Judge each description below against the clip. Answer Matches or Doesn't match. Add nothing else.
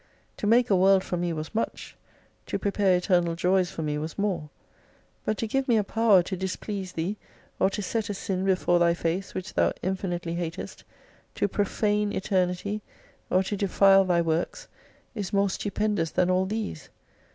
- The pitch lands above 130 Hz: Matches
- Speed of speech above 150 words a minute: Matches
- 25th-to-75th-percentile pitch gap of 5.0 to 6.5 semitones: Doesn't match